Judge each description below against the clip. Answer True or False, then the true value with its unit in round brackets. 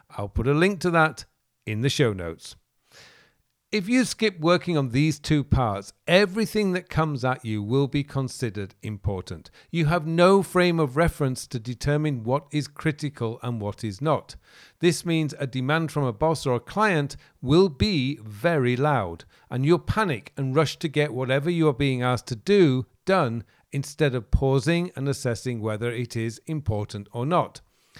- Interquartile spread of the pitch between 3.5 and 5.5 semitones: True (4.9 semitones)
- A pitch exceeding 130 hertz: True (140 Hz)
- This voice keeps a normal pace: True (175 wpm)